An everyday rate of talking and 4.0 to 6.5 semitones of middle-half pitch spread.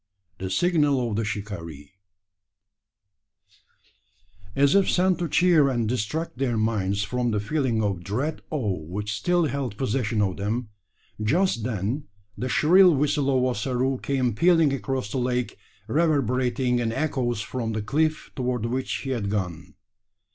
Yes: average, 145 wpm; average, 4.8 semitones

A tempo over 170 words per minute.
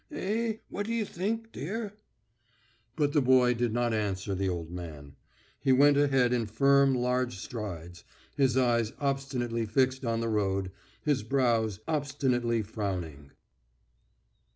No: slow, 135 wpm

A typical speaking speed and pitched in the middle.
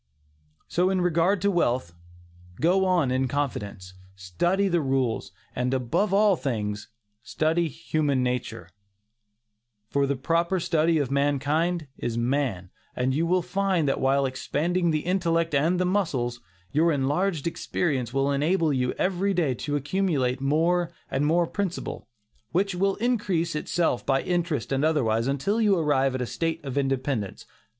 Yes: average, 150 wpm; medium, 150 Hz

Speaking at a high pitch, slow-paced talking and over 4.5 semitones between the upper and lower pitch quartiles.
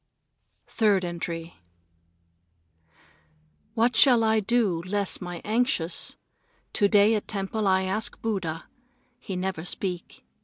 No: high, 195 Hz; slow, 115 wpm; average, 3.7 semitones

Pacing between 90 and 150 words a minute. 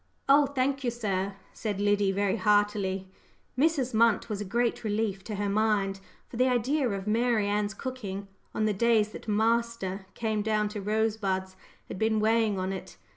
No: average, 175 wpm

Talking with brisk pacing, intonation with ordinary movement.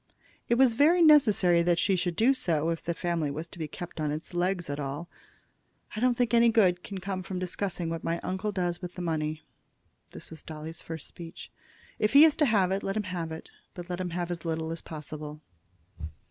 Yes: fast, 220 wpm; average, 3.5 semitones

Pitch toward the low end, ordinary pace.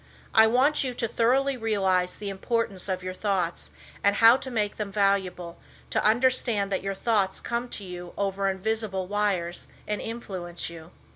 No: high, 200 Hz; average, 165 wpm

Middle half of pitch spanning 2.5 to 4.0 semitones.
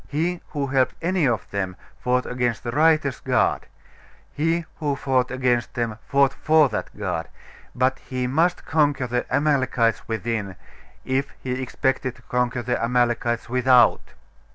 Yes: average, 2.8 semitones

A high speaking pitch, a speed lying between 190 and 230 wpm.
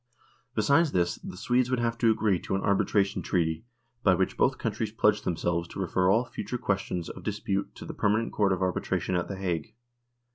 No: low, 100 Hz; average, 195 wpm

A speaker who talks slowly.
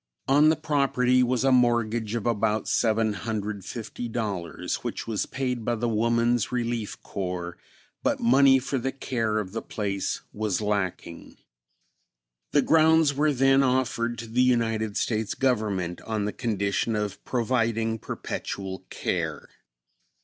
Yes: slow, 130 wpm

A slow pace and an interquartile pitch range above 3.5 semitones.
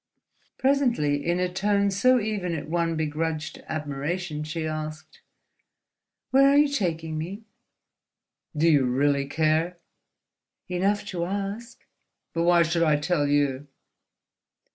Yes: slow, 120 wpm; average, 4.3 semitones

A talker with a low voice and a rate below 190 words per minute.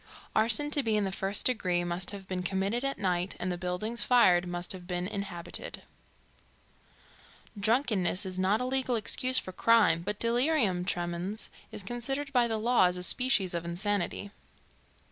No: high, 200 Hz; average, 165 wpm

